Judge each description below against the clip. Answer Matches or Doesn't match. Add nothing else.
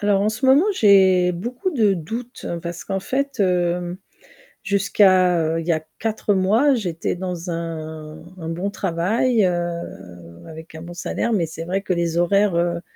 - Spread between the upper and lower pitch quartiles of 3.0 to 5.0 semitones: Matches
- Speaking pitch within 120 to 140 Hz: Doesn't match